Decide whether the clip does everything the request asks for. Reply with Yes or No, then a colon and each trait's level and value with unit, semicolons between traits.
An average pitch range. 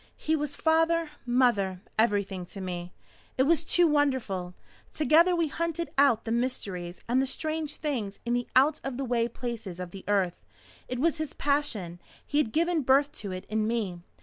No: wide, 7.1 semitones